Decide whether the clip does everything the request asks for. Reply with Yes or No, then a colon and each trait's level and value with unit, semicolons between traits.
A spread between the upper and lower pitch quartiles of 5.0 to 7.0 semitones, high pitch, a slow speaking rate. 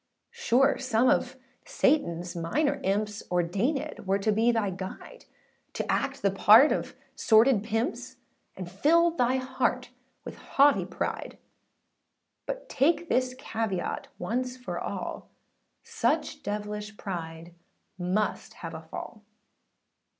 Yes: average, 5.3 semitones; high, 225 Hz; slow, 120 wpm